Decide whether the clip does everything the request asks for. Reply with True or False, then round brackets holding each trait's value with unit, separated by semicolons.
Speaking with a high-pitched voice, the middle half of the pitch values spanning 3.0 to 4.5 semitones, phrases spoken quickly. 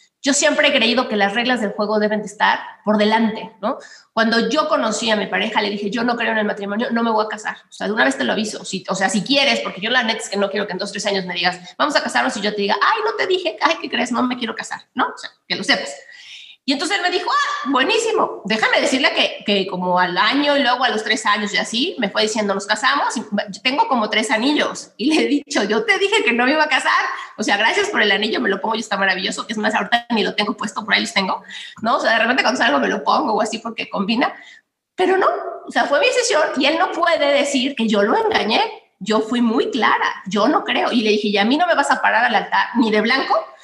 False (230 Hz; 5.6 semitones; 280 wpm)